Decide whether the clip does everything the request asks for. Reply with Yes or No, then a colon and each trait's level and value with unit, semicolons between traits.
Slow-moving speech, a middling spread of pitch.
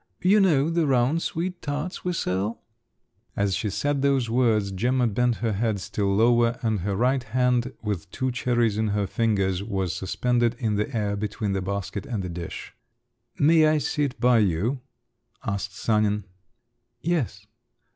No: average, 160 wpm; average, 4.4 semitones